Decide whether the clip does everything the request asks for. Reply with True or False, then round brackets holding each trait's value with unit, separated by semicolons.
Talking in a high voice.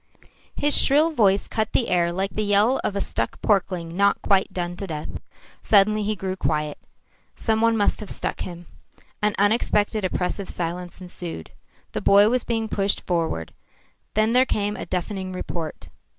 True (200 Hz)